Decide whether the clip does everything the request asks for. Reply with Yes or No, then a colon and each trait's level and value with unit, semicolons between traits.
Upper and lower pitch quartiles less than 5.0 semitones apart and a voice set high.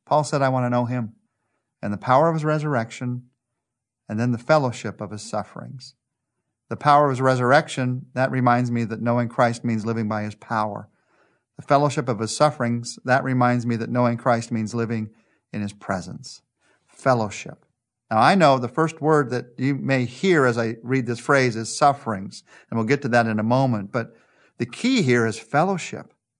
No: average, 2.9 semitones; low, 120 Hz